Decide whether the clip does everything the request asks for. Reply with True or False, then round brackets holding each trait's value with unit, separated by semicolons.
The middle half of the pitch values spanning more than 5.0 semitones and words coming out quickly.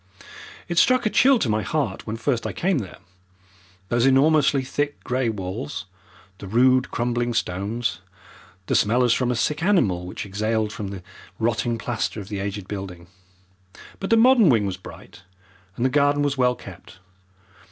False (5.5 semitones; 170 wpm)